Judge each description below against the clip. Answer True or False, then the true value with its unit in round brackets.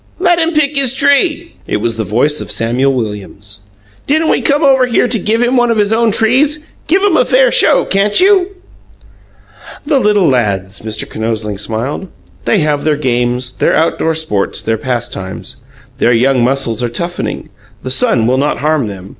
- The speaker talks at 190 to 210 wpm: False (180 wpm)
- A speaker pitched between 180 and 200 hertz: False (150 Hz)